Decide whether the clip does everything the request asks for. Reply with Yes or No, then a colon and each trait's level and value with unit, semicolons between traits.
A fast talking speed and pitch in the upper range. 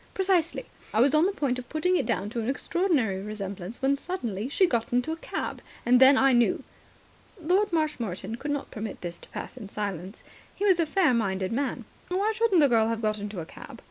Yes: fast, 210 wpm; very high, 250 Hz